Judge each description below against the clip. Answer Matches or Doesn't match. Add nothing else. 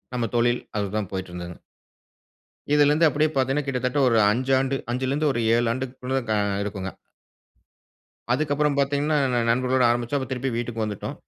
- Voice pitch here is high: Doesn't match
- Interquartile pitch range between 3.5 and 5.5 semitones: Doesn't match